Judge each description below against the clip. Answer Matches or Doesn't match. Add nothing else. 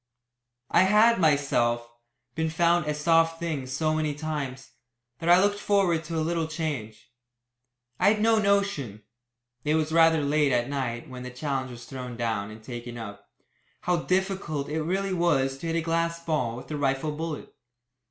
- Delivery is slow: Doesn't match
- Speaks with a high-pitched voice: Doesn't match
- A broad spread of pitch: Doesn't match